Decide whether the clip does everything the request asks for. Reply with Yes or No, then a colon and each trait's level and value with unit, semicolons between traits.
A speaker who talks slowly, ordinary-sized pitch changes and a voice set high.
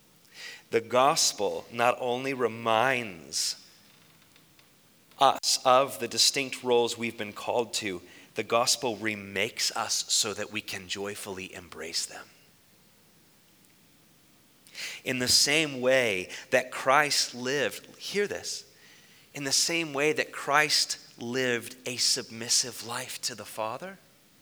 No: slow, 115 wpm; average, 4.0 semitones; low, 120 Hz